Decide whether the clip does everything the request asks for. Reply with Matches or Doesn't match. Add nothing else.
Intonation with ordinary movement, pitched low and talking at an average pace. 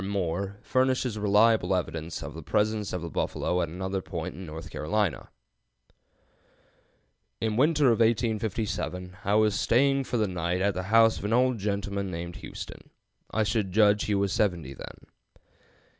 Matches